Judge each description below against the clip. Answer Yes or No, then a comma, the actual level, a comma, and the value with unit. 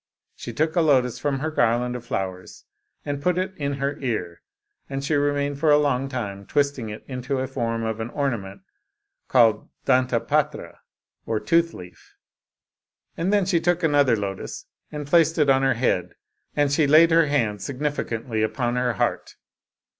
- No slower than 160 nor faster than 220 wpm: Yes, average, 170 wpm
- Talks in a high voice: No, low, 135 Hz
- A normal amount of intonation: Yes, average, 4.3 semitones